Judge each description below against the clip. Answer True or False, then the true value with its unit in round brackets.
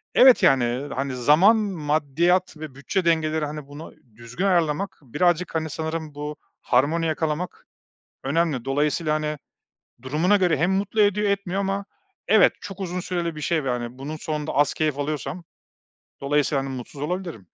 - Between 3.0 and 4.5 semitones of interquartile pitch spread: True (3.9 semitones)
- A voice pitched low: False (155 Hz)